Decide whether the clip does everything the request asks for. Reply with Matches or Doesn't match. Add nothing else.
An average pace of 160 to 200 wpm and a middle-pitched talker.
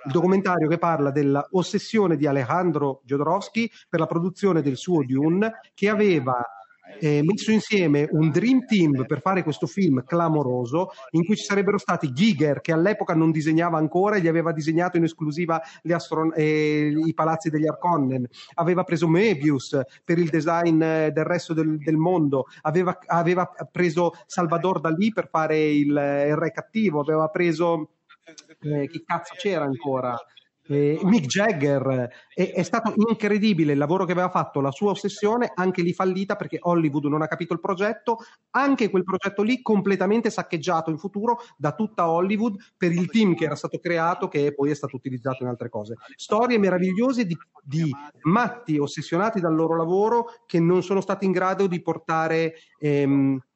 Matches